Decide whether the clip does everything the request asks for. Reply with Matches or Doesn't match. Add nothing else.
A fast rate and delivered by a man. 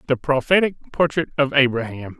Doesn't match